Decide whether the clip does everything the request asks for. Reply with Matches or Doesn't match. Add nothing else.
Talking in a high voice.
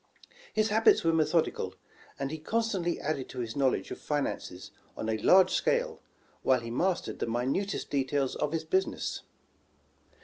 Doesn't match